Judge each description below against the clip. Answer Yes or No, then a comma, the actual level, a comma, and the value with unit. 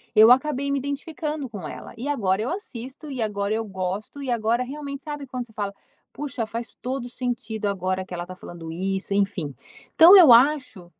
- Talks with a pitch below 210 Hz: No, high, 235 Hz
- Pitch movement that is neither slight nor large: No, wide, 5.8 semitones